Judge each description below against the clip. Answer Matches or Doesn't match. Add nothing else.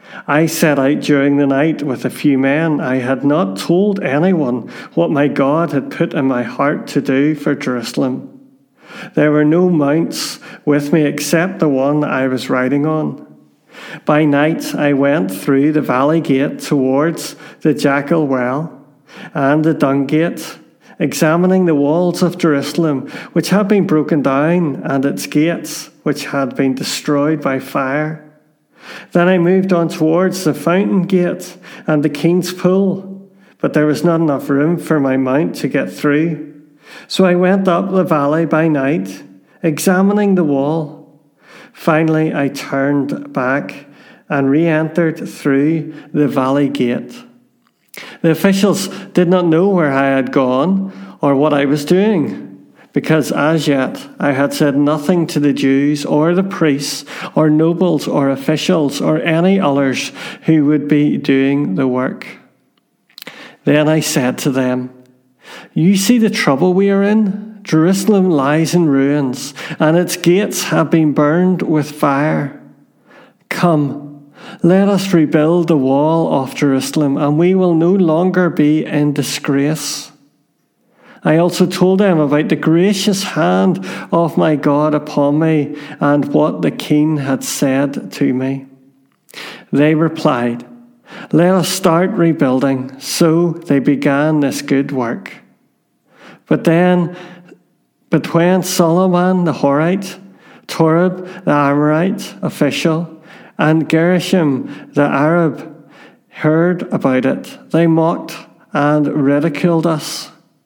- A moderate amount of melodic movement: Matches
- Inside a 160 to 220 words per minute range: Doesn't match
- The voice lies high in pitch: Doesn't match